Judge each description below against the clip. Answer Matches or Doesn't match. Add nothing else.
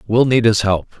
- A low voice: Matches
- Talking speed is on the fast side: Matches